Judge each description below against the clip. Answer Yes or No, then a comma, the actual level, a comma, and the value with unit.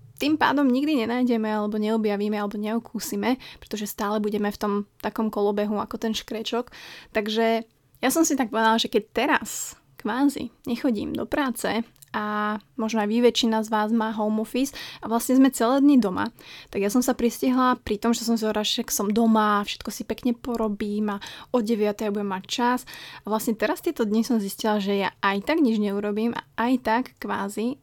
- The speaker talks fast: Yes, fast, 190 wpm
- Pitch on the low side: No, high, 225 Hz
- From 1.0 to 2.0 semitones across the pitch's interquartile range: No, narrow, 2.6 semitones